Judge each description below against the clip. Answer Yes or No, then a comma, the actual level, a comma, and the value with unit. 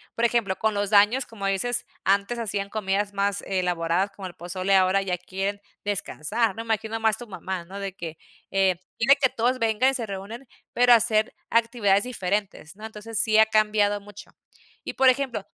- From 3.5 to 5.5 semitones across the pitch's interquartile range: No, average, 2.7 semitones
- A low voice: No, high, 205 Hz